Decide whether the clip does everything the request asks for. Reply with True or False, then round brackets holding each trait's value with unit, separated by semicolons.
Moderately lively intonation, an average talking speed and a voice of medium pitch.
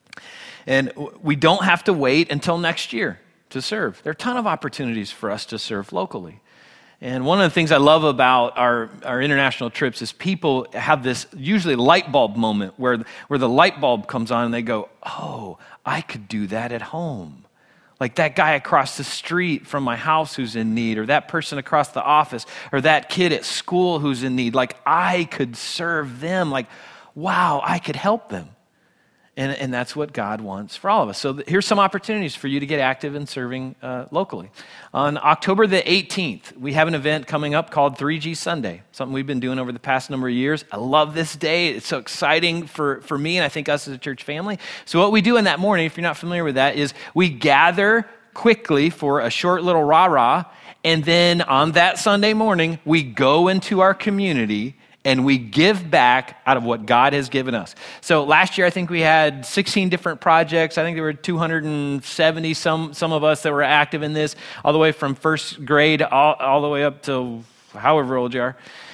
False (4.3 semitones; 215 wpm; 150 Hz)